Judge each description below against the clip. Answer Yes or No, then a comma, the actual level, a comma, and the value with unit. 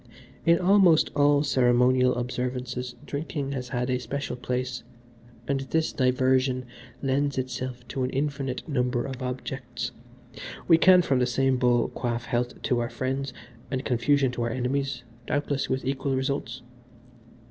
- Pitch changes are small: Yes, narrow, 2.0 semitones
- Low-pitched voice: Yes, low, 130 Hz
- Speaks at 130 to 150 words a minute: Yes, average, 145 wpm